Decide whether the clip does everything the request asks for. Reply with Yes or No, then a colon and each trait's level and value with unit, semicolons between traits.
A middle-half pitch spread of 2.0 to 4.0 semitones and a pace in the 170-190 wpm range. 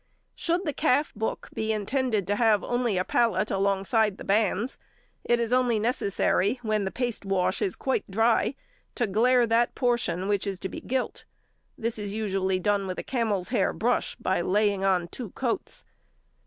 Yes: average, 3.7 semitones; average, 175 wpm